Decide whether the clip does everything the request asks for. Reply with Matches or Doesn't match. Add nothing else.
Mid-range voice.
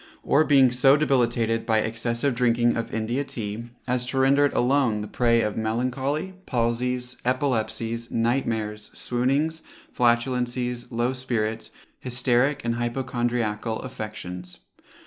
Doesn't match